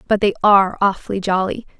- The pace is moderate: Yes, average, 165 wpm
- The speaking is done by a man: No, female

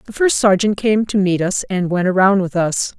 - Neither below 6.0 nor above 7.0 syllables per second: No, 5.0 syllables/s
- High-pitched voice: Yes, high, 195 Hz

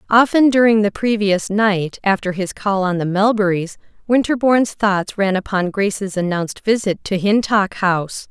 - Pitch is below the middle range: No, high, 200 Hz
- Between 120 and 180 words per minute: Yes, average, 150 wpm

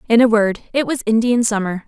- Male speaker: No, female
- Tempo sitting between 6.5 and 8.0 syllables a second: No, 5.7 syllables/s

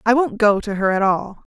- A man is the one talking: No, female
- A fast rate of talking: Yes, fast, 270 wpm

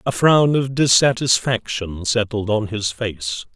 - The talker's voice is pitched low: Yes, low, 115 Hz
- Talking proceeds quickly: No, slow, 135 wpm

